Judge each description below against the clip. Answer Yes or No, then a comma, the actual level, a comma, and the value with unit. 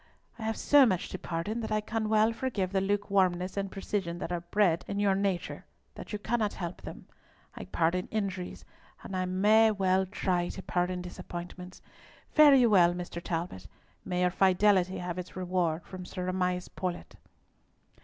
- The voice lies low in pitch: No, medium, 185 Hz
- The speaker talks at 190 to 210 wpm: No, average, 175 wpm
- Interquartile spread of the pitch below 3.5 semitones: Yes, narrow, 2.5 semitones